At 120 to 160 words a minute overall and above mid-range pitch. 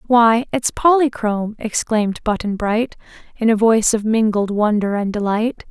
Yes: average, 145 wpm; high, 220 Hz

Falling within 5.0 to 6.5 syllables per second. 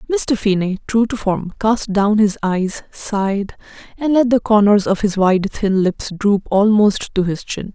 No: 4.1 syllables/s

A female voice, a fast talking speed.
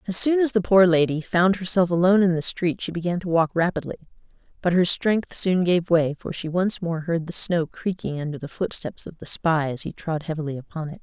Yes: female; fast, 235 wpm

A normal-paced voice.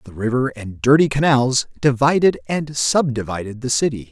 Yes: average, 145 wpm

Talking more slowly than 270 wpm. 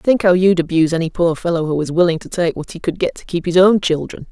No: fast, 290 wpm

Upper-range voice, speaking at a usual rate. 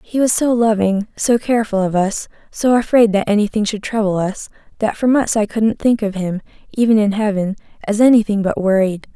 Yes: high, 215 Hz; average, 195 wpm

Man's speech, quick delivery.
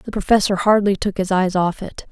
No: female; fast, 225 wpm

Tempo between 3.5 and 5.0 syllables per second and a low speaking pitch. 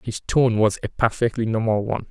No: 5.6 syllables/s; low, 115 Hz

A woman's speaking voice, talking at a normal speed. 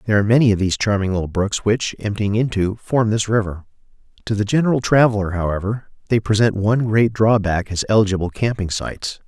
No: male; average, 180 wpm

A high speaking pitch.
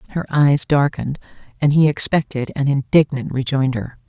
No: medium, 140 Hz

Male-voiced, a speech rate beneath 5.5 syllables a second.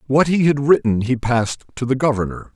No: male; 5.7 syllables/s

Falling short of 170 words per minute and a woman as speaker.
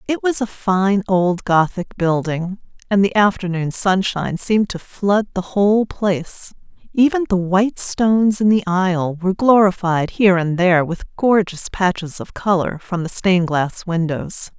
Yes: average, 160 wpm; female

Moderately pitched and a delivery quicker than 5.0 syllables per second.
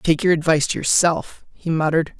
Yes: medium, 160 Hz; 5.8 syllables/s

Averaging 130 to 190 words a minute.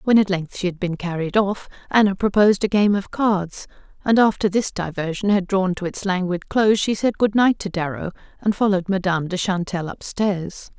No: average, 200 wpm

